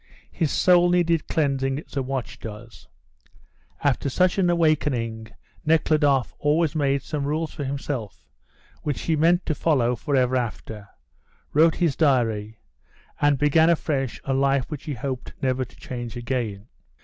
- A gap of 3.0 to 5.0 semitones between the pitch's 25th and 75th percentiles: Yes, average, 4.1 semitones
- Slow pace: No, average, 145 wpm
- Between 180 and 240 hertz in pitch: No, medium, 140 Hz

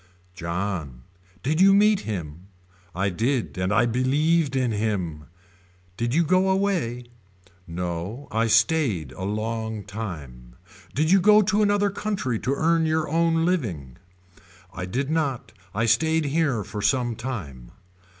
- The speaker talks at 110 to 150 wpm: Yes, average, 140 wpm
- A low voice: Yes, low, 120 Hz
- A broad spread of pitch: Yes, wide, 8.9 semitones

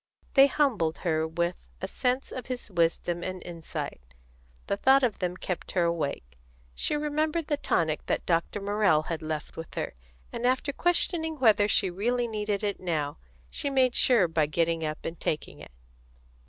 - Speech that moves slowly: No, average, 170 wpm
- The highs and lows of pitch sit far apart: Yes, wide, 7.6 semitones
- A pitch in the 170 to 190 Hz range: Yes, medium, 185 Hz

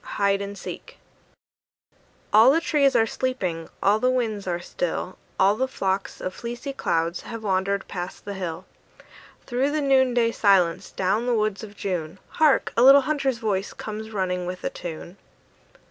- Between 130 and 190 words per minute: Yes, average, 160 wpm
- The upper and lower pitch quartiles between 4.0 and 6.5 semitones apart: Yes, average, 5.2 semitones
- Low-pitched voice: No, high, 210 Hz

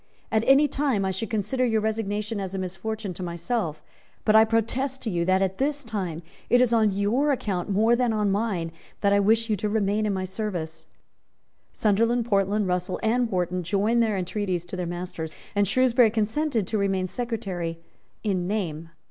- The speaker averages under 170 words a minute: No, average, 185 wpm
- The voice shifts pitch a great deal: No, average, 3.5 semitones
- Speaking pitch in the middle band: No, high, 205 Hz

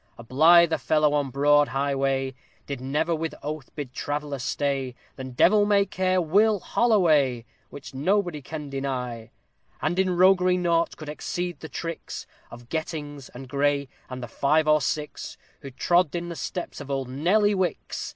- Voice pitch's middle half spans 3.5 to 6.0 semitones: Yes, average, 4.1 semitones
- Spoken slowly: No, average, 165 wpm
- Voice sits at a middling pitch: Yes, medium, 150 Hz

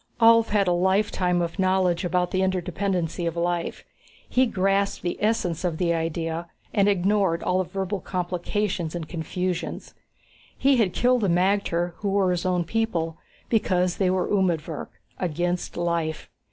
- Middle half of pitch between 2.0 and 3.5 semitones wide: Yes, narrow, 2.4 semitones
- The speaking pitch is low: No, medium, 180 Hz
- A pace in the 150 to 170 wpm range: Yes, average, 155 wpm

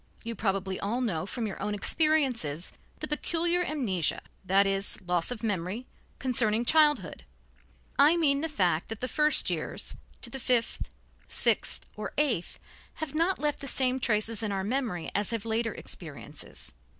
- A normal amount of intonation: No, wide, 6.3 semitones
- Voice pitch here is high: Yes, high, 230 Hz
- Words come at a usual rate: Yes, average, 160 wpm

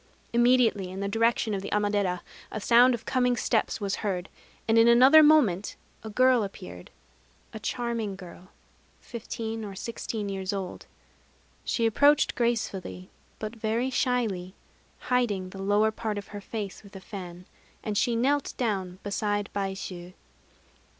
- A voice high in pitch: Yes, high, 210 Hz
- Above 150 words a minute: No, average, 145 wpm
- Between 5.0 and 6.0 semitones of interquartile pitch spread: No, average, 3.4 semitones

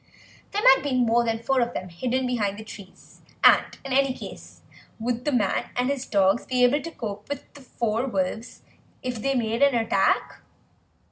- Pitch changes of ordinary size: Yes, average, 3.1 semitones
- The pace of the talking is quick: No, average, 190 wpm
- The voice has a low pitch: No, high, 245 Hz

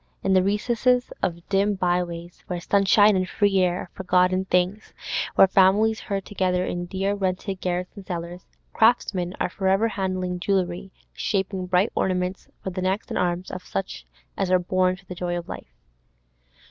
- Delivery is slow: No, average, 170 wpm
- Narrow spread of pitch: Yes, narrow, 1.5 semitones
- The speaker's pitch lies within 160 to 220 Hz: Yes, medium, 185 Hz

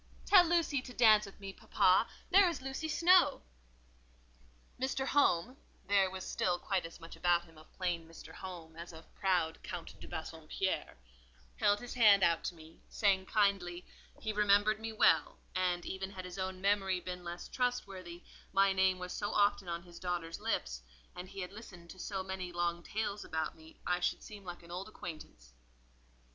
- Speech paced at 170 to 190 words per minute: Yes, average, 180 wpm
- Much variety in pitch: No, average, 3.1 semitones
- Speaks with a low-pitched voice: No, medium, 185 Hz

